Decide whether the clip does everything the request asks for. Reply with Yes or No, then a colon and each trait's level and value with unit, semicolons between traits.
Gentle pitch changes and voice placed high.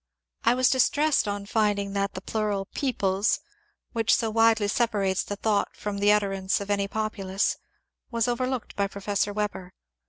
Yes: narrow, 2.3 semitones; high, 210 Hz